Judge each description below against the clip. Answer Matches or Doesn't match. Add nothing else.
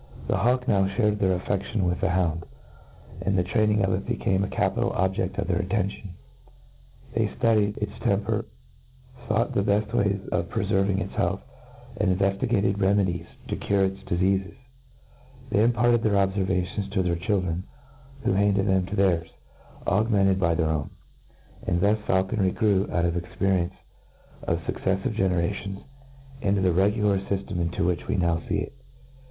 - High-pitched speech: Doesn't match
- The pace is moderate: Matches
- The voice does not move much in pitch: Matches